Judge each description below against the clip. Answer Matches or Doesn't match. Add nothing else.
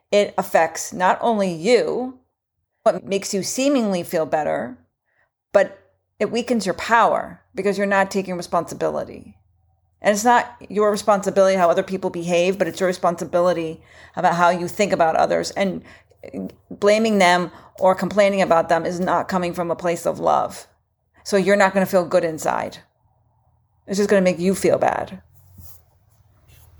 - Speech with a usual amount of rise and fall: Matches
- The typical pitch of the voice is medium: Matches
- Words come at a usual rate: Matches